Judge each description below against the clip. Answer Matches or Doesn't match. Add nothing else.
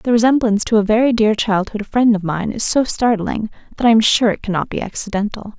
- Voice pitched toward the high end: Matches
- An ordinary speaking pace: Doesn't match